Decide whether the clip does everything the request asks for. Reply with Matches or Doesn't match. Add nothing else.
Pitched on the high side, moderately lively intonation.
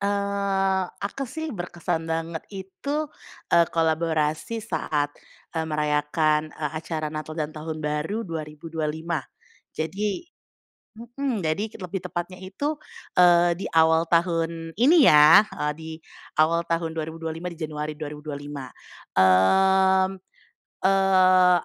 Doesn't match